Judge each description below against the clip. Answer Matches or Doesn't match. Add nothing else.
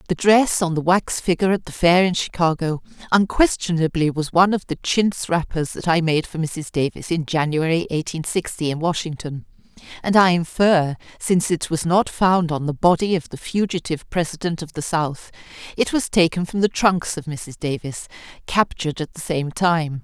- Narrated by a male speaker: Doesn't match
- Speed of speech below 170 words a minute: Doesn't match